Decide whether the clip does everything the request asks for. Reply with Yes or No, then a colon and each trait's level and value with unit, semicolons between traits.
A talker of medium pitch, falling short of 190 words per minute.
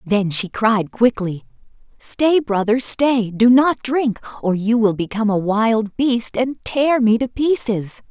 No: high, 230 Hz; average, 165 wpm